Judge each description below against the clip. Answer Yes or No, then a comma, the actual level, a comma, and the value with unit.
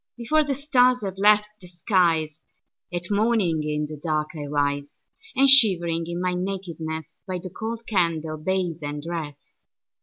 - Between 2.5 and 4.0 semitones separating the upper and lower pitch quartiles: No, average, 5.1 semitones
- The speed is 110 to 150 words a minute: Yes, average, 140 wpm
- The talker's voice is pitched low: No, medium, 175 Hz